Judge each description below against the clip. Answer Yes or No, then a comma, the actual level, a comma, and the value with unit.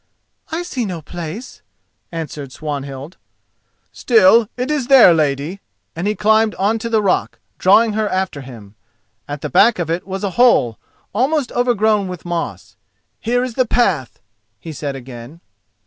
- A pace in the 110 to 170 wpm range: Yes, average, 155 wpm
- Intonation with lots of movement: Yes, wide, 6.9 semitones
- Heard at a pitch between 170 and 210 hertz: Yes, high, 190 Hz